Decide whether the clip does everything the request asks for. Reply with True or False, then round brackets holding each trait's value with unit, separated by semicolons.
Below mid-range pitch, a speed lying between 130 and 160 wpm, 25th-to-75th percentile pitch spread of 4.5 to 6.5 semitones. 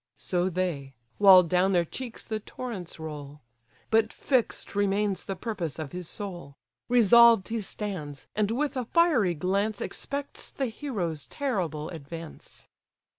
False (195 Hz; 135 wpm; 5.3 semitones)